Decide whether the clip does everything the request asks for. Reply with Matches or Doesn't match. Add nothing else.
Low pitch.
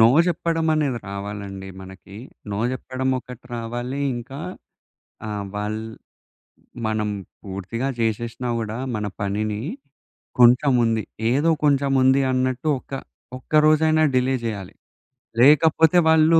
Matches